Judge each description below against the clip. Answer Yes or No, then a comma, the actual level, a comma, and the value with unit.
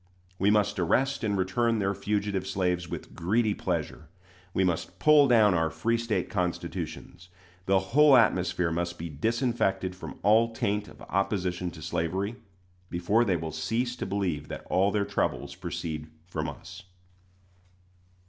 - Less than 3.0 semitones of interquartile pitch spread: No, average, 3.8 semitones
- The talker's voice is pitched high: No, very low, 95 Hz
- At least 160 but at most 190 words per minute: No, average, 150 wpm